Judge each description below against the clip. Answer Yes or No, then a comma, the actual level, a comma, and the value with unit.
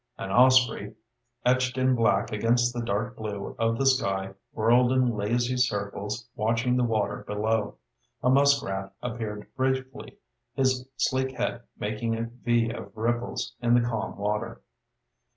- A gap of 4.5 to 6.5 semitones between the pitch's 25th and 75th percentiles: No, average, 3.0 semitones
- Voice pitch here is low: Yes, low, 115 Hz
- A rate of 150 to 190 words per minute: No, average, 140 wpm